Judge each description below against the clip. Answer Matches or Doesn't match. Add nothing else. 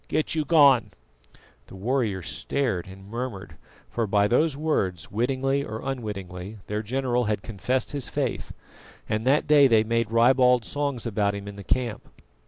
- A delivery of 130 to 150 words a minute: Doesn't match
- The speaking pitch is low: Matches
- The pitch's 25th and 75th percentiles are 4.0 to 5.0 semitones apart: Matches